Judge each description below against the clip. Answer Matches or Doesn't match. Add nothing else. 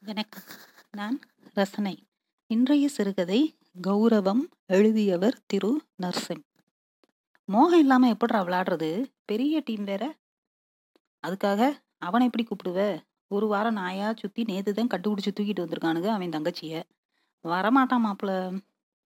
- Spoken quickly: Doesn't match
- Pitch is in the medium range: Doesn't match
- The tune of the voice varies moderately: Matches